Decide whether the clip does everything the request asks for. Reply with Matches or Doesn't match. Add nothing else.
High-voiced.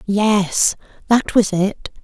Matches